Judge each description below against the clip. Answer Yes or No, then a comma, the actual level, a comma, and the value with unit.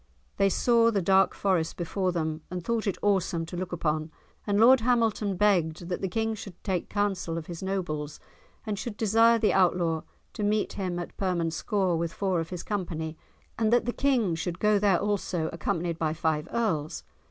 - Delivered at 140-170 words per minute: No, average, 185 wpm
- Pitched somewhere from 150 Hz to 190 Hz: Yes, medium, 185 Hz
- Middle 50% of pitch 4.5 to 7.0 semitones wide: No, average, 3.9 semitones